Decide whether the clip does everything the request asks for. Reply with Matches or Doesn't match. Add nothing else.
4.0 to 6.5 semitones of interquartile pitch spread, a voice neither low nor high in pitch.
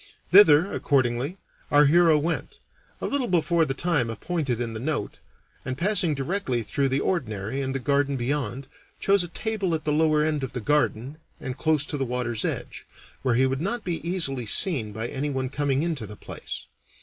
Matches